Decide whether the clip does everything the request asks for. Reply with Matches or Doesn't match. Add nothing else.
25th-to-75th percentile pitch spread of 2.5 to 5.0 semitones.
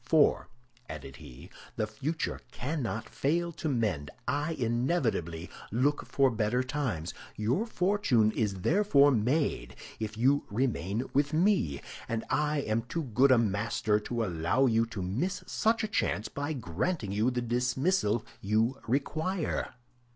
Doesn't match